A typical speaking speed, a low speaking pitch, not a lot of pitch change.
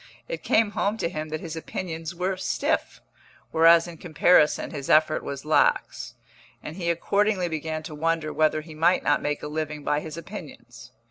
No: average, 180 wpm; medium, 160 Hz; narrow, 2.3 semitones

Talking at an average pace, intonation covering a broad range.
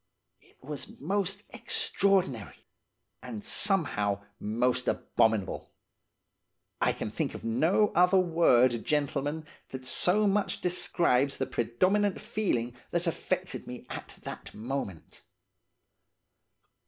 No: slow, 105 wpm; wide, 7.4 semitones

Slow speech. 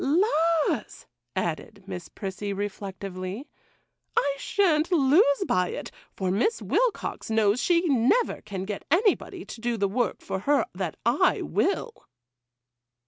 Yes: slow, 130 wpm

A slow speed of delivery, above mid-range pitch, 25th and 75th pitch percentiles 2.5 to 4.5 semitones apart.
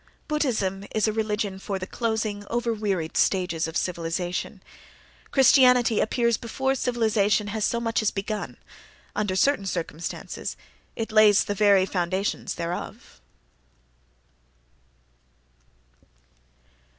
Yes: slow, 100 wpm; high, 210 Hz; average, 3.2 semitones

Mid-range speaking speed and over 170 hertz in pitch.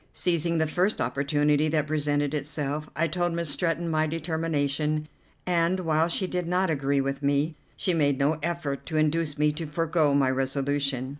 No: average, 170 wpm; medium, 155 Hz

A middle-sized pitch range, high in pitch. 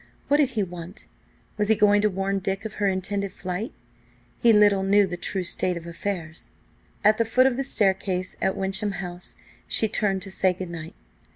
No: narrow, 2.3 semitones; high, 195 Hz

